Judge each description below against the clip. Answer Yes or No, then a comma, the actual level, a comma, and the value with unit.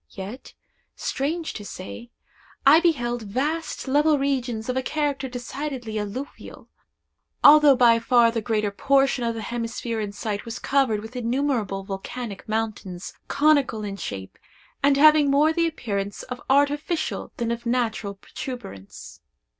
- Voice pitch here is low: No, high, 245 Hz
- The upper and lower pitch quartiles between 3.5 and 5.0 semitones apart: Yes, average, 4.5 semitones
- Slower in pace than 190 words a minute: Yes, average, 140 wpm